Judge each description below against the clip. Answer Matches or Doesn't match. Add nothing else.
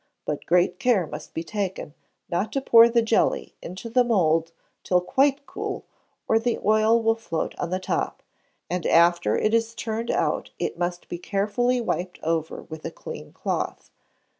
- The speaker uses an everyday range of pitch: Matches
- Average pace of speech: Matches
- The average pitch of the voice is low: Doesn't match